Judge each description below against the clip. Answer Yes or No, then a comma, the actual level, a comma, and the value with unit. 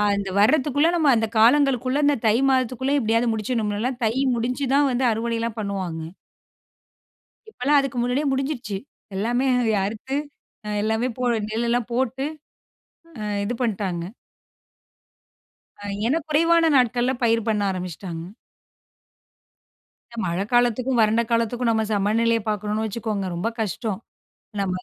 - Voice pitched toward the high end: Yes, high, 230 Hz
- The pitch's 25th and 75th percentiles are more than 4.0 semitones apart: No, average, 3.3 semitones